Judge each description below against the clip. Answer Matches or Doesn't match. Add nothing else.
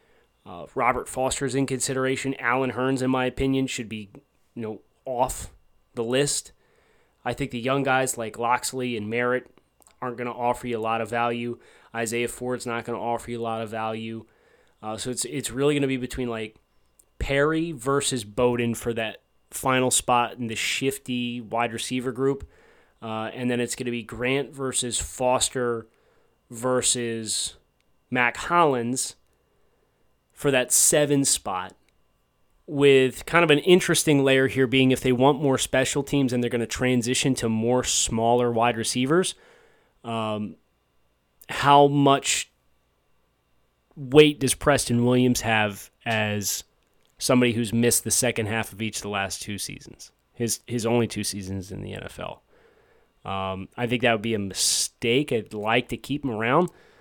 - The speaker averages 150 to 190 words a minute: Matches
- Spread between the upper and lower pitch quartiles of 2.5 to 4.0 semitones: Matches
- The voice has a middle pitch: Doesn't match